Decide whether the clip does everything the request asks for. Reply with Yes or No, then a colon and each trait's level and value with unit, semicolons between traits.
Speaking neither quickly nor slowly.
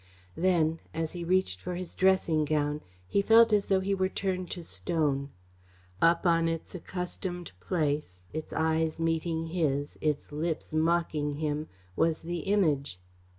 Yes: average, 150 wpm